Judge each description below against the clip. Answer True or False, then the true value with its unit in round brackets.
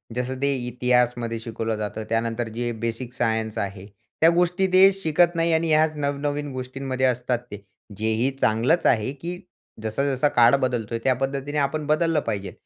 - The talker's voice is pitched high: False (130 Hz)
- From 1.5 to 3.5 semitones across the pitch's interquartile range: False (4.5 semitones)